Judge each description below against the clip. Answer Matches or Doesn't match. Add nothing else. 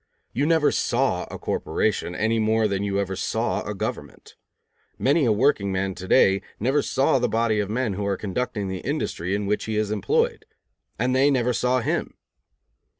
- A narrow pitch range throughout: Doesn't match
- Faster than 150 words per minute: Matches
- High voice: Doesn't match